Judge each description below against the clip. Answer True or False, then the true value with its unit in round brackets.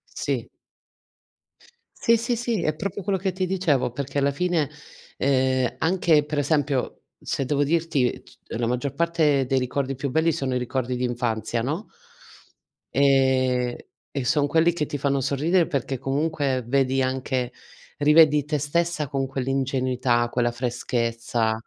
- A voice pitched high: False (140 Hz)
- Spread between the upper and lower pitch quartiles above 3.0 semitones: True (3.5 semitones)